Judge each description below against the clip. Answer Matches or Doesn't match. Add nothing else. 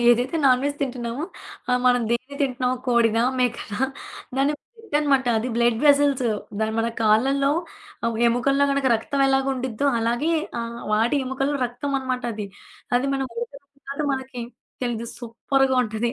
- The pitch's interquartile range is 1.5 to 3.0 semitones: Matches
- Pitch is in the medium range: Doesn't match